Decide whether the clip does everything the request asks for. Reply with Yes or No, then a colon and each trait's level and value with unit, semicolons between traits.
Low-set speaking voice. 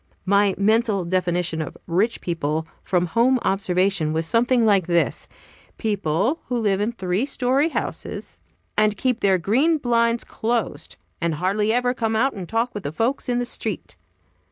No: high, 205 Hz